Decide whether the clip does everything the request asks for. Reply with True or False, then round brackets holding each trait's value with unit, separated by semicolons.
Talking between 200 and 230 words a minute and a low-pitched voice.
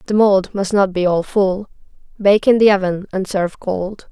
False (205 wpm; 195 Hz)